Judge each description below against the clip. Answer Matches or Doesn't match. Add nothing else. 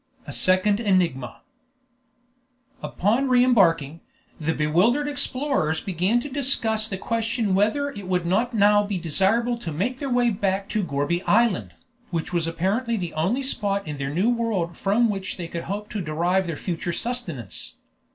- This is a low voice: Doesn't match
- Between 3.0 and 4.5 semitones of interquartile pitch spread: Doesn't match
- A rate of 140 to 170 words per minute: Matches